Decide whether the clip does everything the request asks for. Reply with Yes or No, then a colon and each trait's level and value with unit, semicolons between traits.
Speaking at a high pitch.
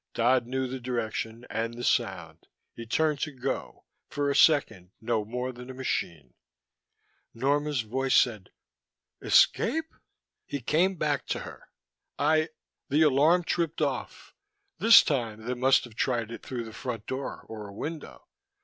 No: low, 130 Hz